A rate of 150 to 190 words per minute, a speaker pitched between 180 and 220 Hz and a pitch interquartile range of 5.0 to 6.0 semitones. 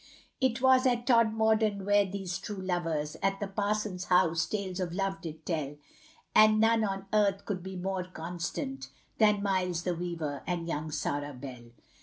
No: average, 165 wpm; high, 190 Hz; average, 3.9 semitones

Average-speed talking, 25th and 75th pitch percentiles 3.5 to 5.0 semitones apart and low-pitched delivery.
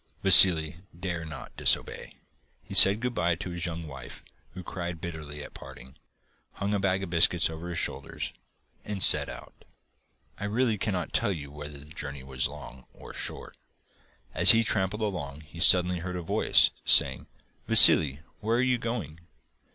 Yes: average, 165 wpm; average, 4.3 semitones; very low, 85 Hz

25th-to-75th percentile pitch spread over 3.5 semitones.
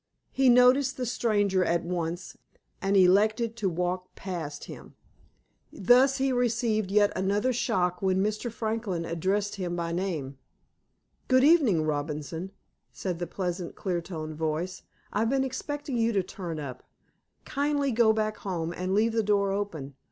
Yes: average, 4.9 semitones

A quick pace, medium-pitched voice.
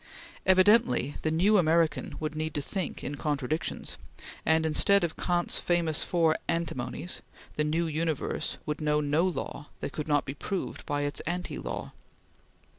No: average, 155 wpm; medium, 160 Hz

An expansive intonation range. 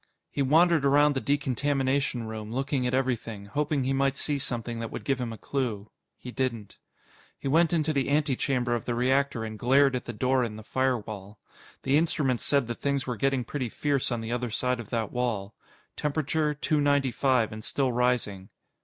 No: average, 3.2 semitones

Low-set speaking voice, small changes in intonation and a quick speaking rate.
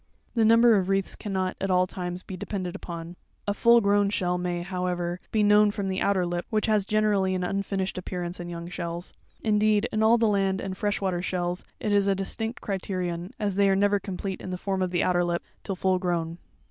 No: high, 190 Hz; narrow, 2.3 semitones; fast, 220 wpm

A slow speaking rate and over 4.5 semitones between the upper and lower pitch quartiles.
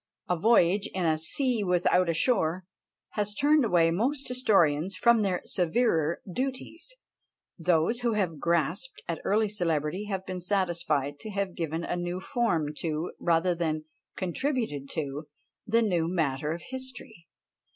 No: average, 145 wpm; average, 5.1 semitones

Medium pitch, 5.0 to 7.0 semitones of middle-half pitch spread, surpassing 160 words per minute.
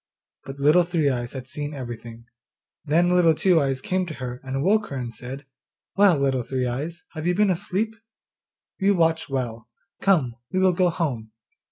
Yes: medium, 145 Hz; wide, 5.6 semitones; average, 180 wpm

